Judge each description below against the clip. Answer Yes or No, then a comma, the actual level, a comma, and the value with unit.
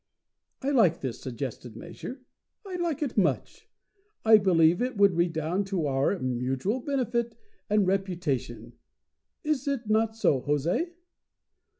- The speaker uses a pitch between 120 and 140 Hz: No, high, 190 Hz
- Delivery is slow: Yes, slow, 125 wpm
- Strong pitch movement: Yes, wide, 8.5 semitones